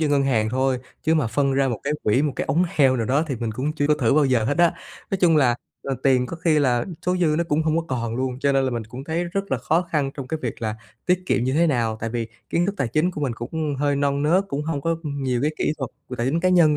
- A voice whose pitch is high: No, medium, 140 Hz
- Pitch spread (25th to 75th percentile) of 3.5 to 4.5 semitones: Yes, average, 4.0 semitones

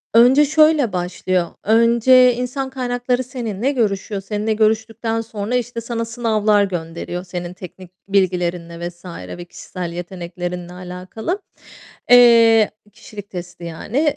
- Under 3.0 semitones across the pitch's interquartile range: No, average, 5.2 semitones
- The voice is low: No, high, 215 Hz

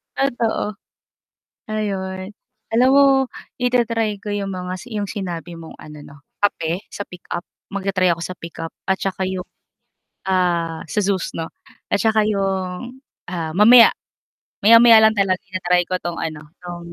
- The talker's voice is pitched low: No, high, 190 Hz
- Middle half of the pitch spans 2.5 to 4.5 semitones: Yes, average, 3.3 semitones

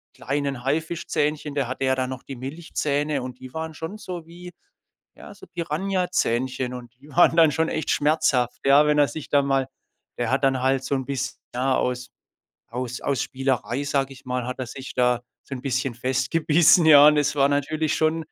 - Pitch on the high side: No, medium, 140 Hz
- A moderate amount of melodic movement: Yes, average, 3.2 semitones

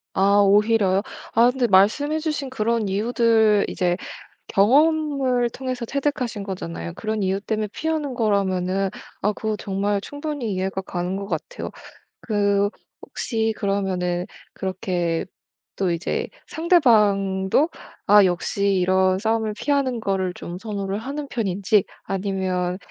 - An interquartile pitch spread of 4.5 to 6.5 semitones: No, average, 3.9 semitones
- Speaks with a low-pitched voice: No, high, 205 Hz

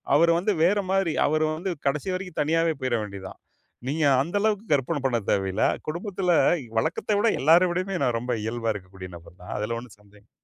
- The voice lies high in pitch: No, medium, 150 Hz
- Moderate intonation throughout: No, wide, 8.2 semitones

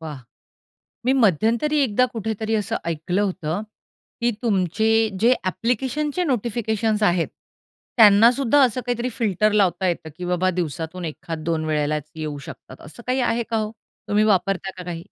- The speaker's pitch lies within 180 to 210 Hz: Yes, high, 205 Hz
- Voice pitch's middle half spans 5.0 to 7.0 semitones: Yes, wide, 5.4 semitones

